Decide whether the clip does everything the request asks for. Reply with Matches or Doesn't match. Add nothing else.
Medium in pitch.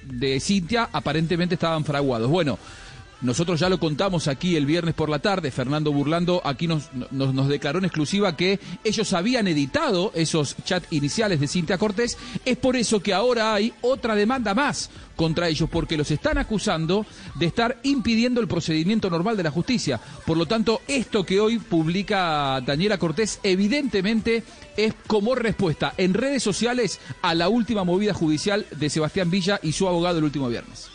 Matches